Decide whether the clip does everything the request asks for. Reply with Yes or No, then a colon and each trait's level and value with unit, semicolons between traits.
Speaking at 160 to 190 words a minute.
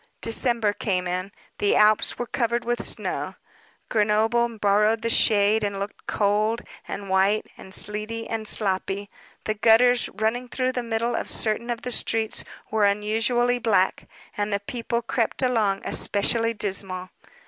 No: average, 150 wpm